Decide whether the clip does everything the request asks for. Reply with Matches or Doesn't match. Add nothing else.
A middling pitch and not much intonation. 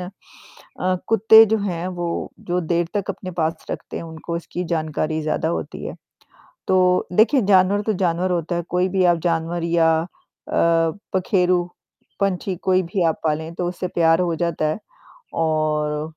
Matches